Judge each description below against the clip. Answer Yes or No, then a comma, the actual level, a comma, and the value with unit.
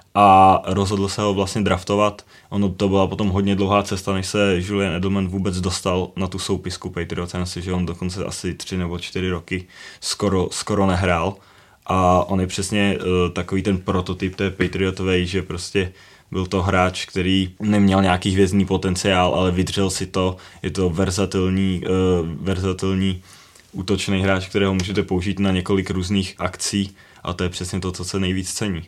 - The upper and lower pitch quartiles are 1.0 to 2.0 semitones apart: Yes, narrow, 1.3 semitones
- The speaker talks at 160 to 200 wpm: Yes, fast, 170 wpm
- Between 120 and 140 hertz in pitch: No, very low, 95 Hz